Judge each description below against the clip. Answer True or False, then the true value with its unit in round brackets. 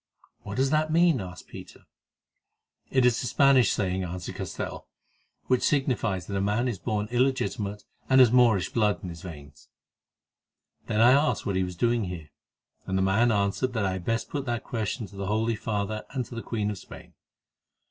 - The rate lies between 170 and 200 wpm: True (190 wpm)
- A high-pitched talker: False (110 Hz)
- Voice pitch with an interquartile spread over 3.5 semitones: True (4.4 semitones)